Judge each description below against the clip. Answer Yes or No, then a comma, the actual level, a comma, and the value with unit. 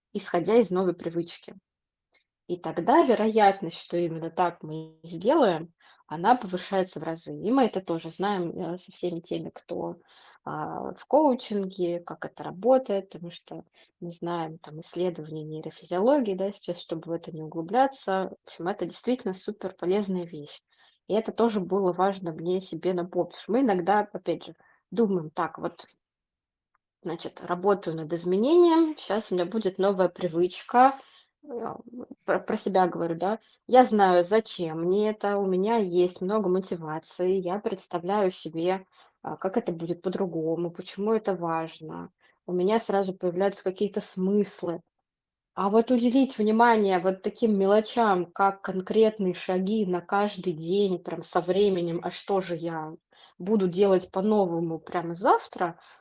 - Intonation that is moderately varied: Yes, average, 3.2 semitones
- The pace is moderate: Yes, average, 140 wpm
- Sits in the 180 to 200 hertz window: Yes, medium, 185 Hz